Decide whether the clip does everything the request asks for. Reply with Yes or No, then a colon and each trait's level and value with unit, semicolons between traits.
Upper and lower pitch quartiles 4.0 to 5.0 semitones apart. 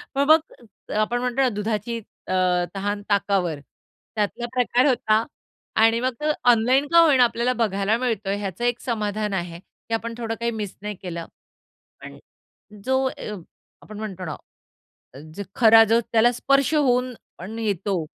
No: average, 3.4 semitones